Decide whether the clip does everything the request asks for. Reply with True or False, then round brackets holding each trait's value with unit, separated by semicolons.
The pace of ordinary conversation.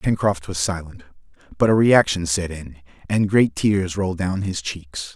True (175 wpm)